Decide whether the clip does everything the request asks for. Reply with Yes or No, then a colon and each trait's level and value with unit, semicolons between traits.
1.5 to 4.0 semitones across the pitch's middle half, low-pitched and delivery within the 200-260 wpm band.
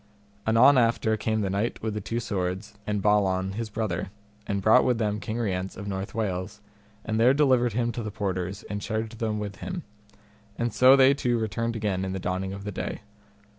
Yes: average, 3.0 semitones; low, 110 Hz; fast, 205 wpm